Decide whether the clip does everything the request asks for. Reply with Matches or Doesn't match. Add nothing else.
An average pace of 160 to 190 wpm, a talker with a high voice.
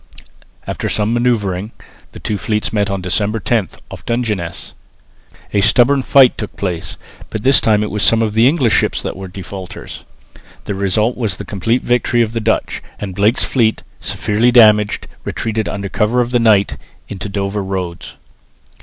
Doesn't match